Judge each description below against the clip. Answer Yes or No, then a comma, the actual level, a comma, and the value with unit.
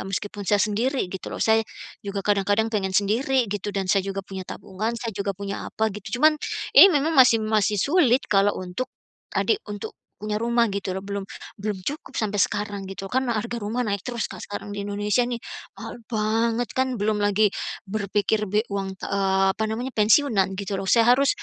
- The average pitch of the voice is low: No, high, 210 Hz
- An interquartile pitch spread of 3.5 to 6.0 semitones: No, average, 2.9 semitones